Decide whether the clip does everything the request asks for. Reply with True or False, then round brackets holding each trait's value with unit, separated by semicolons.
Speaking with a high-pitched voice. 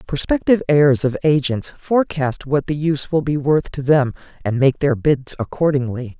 False (145 Hz)